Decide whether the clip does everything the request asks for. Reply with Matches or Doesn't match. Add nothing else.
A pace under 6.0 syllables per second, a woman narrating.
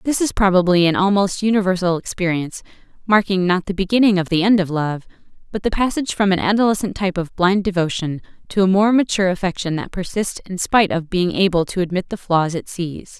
Doesn't match